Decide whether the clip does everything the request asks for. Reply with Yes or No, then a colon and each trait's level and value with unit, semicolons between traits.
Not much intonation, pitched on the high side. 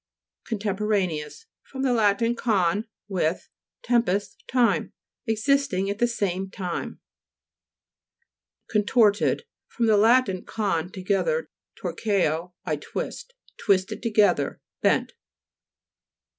No: average, 3.8 semitones; high, 210 Hz